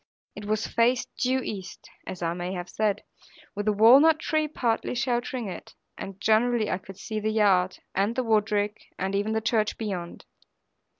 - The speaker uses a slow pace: No, average, 170 wpm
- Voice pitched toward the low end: No, high, 215 Hz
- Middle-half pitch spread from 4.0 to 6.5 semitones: No, average, 3.5 semitones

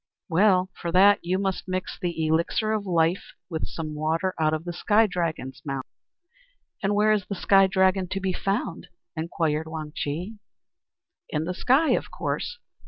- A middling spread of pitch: Yes, average, 3.4 semitones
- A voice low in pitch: No, medium, 180 Hz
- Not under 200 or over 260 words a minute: No, average, 170 wpm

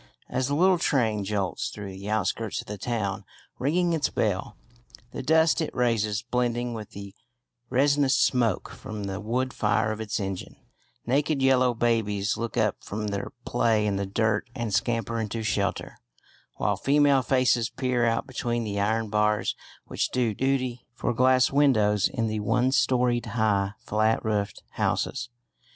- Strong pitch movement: No, average, 3.4 semitones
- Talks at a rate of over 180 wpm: No, average, 160 wpm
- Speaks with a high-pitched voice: No, low, 115 Hz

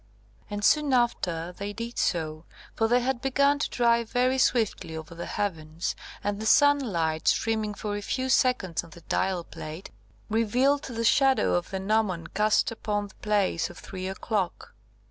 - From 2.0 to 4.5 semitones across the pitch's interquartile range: No, average, 5.2 semitones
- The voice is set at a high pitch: Yes, high, 210 Hz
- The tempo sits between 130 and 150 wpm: No, average, 165 wpm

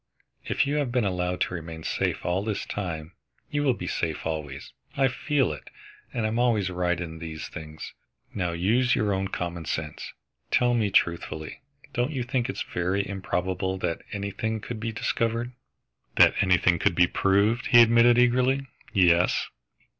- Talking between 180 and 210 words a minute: No, average, 170 wpm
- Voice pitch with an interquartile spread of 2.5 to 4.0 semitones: No, wide, 5.6 semitones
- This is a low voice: Yes, low, 100 Hz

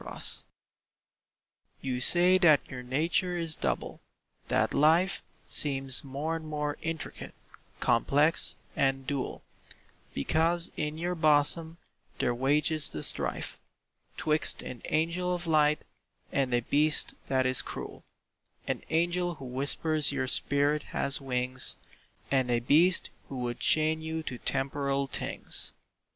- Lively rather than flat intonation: No, average, 3.3 semitones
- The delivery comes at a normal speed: No, slow, 125 wpm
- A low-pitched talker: No, medium, 150 Hz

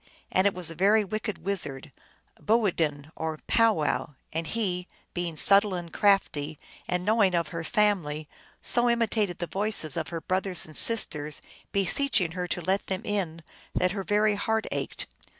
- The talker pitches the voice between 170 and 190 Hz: Yes, medium, 185 Hz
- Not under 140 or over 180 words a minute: Yes, average, 170 wpm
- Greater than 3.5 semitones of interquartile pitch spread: Yes, average, 4.1 semitones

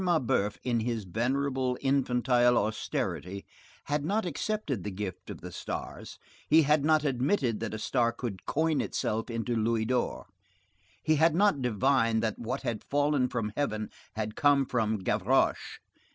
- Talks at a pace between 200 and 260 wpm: No, average, 150 wpm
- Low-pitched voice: Yes, low, 125 Hz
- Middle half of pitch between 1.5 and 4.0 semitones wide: No, average, 4.4 semitones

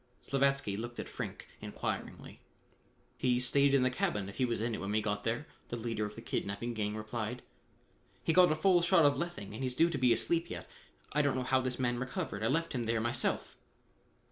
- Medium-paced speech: No, fast, 220 wpm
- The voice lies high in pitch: No, low, 125 Hz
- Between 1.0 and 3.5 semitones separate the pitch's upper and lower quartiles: No, average, 4.0 semitones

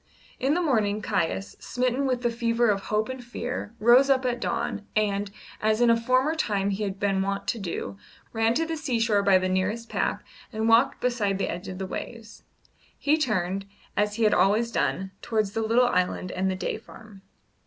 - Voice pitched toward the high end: Yes, high, 220 Hz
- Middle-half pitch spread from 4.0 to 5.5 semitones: No, average, 3.5 semitones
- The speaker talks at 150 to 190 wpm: No, average, 200 wpm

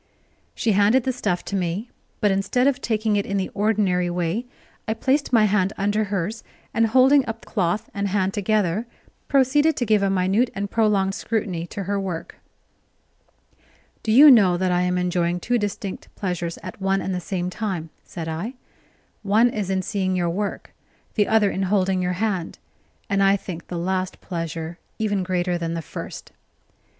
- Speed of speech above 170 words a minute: Yes, average, 180 wpm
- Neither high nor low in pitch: No, high, 195 Hz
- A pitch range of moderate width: Yes, average, 3.3 semitones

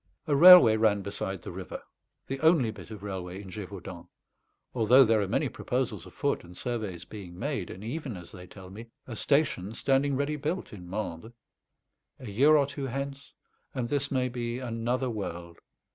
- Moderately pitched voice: No, low, 115 Hz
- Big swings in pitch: Yes, wide, 5.9 semitones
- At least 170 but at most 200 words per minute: Yes, average, 175 wpm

